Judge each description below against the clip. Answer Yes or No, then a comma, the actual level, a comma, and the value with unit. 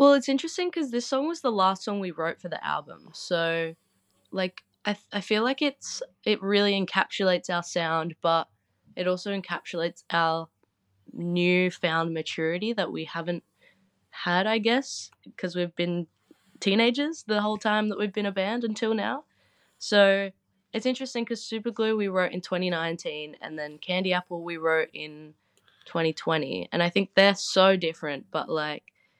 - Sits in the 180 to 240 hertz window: Yes, medium, 185 Hz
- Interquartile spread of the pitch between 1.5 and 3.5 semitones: No, average, 4.4 semitones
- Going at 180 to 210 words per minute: No, average, 165 wpm